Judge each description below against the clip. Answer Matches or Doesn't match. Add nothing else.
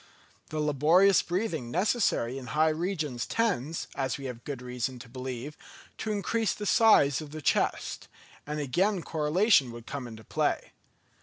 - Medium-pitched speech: Matches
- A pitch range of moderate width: Doesn't match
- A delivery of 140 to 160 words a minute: Matches